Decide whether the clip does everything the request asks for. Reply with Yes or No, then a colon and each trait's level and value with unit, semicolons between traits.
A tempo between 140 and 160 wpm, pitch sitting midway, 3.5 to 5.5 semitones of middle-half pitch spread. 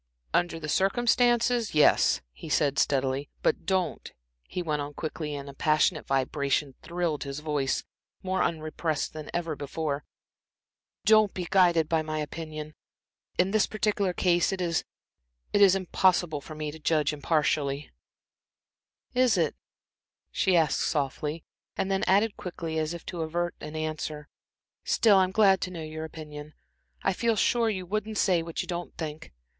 Yes: average, 150 wpm; medium, 160 Hz; average, 3.8 semitones